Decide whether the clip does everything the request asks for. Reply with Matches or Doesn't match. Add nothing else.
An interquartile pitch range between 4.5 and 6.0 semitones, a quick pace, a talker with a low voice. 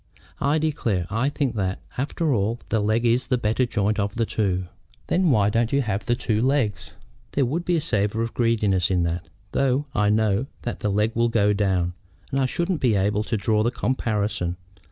Doesn't match